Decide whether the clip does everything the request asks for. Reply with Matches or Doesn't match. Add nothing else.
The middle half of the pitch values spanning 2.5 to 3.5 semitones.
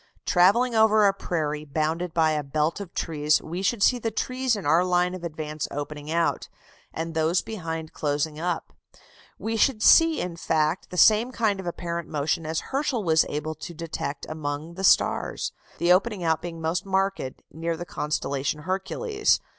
Doesn't match